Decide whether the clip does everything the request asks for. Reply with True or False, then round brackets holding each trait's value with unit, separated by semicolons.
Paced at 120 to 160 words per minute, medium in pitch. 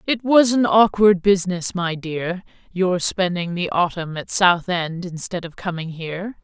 False (170 wpm; 180 Hz)